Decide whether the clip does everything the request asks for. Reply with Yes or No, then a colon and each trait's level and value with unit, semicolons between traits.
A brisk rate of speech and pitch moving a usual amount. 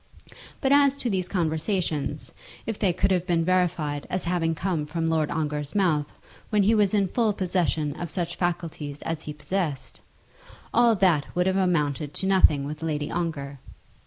No: average, 170 wpm; average, 4.0 semitones